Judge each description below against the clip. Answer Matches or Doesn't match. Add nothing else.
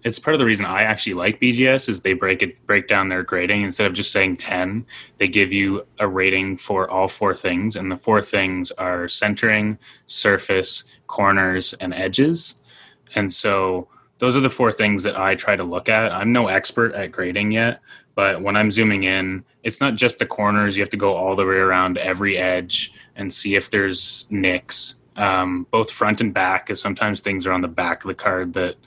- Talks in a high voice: Doesn't match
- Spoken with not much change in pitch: Matches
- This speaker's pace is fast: Matches